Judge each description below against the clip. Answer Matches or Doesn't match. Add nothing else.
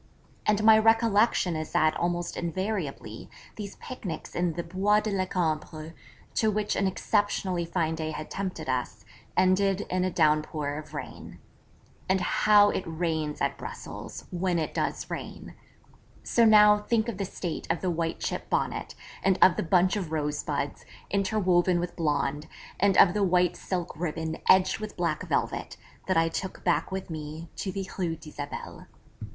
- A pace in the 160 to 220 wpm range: Matches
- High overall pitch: Doesn't match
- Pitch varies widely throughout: Doesn't match